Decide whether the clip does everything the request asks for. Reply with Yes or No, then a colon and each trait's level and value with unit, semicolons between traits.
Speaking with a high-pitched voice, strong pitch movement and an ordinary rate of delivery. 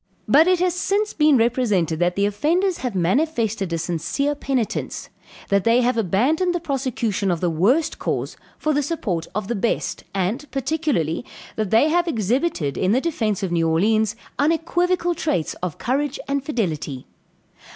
Yes: high, 240 Hz; wide, 8.3 semitones; average, 160 wpm